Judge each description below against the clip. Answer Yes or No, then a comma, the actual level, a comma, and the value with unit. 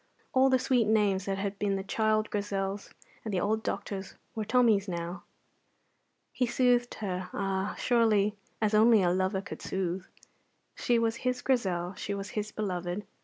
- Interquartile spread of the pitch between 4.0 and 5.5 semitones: No, average, 2.7 semitones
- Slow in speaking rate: No, average, 165 wpm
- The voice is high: Yes, high, 205 Hz